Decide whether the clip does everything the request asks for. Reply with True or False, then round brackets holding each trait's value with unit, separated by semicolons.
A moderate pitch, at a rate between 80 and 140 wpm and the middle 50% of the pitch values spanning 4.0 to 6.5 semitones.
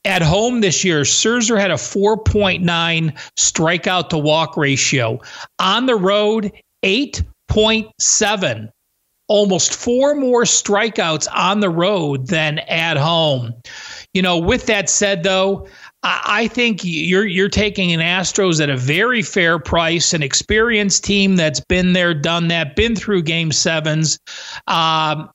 True (180 Hz; 135 wpm; 4.5 semitones)